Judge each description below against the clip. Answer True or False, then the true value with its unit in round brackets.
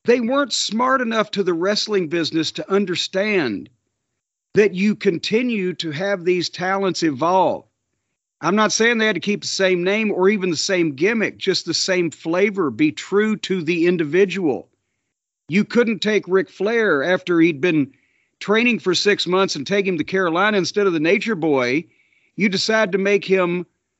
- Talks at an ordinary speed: True (175 wpm)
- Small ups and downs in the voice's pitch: False (3.0 semitones)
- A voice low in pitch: False (190 Hz)